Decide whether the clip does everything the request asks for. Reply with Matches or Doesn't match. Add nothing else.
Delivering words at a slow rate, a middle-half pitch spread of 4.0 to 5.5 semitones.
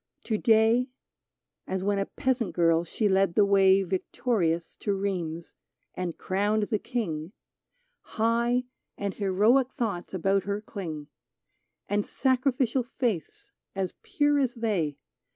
Matches